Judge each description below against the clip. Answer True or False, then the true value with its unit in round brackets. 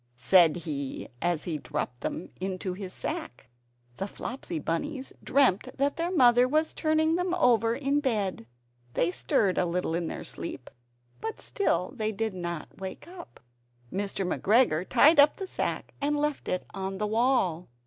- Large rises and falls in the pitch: True (8.2 semitones)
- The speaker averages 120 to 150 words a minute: False (160 wpm)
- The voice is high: True (210 Hz)